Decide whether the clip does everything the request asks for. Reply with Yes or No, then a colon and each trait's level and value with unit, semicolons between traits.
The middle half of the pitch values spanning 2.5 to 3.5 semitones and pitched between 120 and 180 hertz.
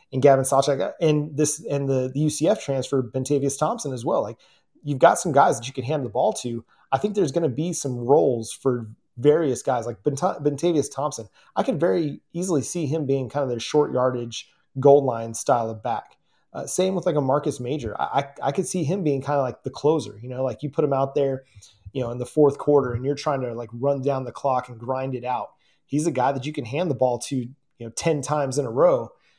Yes: average, 2.9 semitones; medium, 140 Hz